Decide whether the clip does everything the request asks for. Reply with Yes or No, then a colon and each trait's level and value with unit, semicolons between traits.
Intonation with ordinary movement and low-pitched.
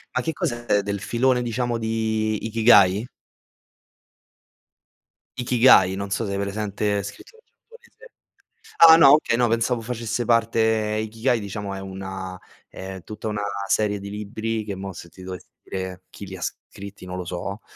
Yes: average, 3.2 semitones; low, 105 Hz